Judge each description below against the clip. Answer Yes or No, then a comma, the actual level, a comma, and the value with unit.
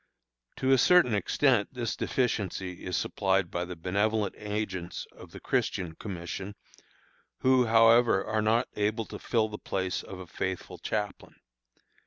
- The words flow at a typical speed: Yes, average, 145 wpm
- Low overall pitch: Yes, low, 105 Hz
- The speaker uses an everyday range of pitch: Yes, average, 3.5 semitones